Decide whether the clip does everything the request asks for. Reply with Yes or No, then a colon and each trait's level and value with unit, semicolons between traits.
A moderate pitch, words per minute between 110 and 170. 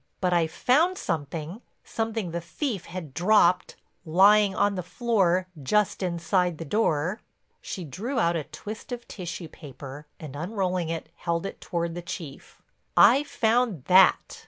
Yes: medium, 180 Hz; average, 150 wpm